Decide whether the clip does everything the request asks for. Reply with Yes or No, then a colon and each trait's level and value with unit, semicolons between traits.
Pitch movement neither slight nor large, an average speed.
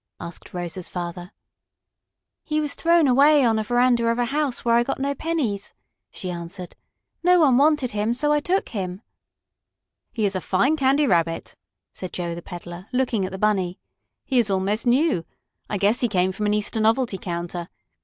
No: wide, 6.4 semitones; average, 185 wpm